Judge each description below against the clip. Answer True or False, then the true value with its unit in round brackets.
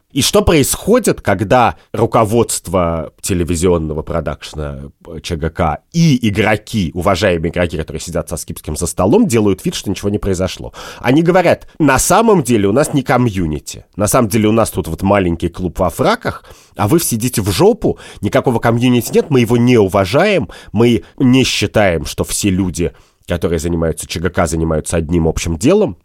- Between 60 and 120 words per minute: False (160 wpm)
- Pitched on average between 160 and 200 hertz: False (95 Hz)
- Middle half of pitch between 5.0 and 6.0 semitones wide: True (5.6 semitones)